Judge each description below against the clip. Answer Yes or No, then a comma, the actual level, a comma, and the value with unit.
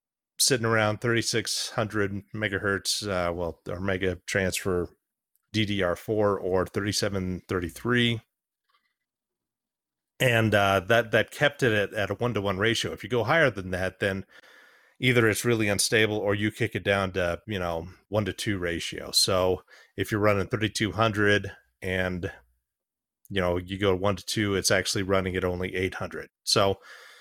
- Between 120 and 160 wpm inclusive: Yes, average, 150 wpm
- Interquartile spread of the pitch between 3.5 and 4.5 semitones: No, average, 2.7 semitones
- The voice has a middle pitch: No, low, 100 Hz